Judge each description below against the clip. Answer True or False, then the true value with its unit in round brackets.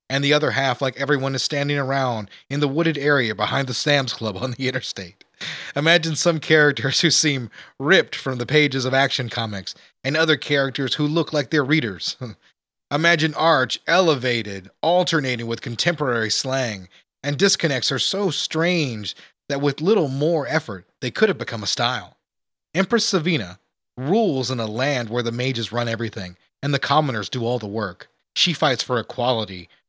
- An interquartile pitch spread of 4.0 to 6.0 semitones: True (4.6 semitones)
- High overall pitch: False (135 Hz)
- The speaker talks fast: False (170 wpm)